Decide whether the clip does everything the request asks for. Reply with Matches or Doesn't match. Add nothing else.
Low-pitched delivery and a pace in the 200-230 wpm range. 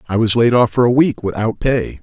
Doesn't match